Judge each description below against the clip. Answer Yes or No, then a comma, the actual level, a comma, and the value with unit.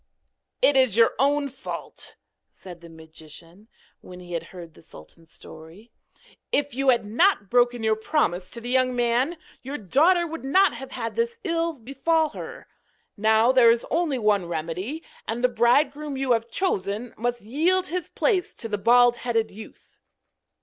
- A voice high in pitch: Yes, high, 240 Hz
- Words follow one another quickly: No, average, 165 wpm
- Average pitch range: No, wide, 5.8 semitones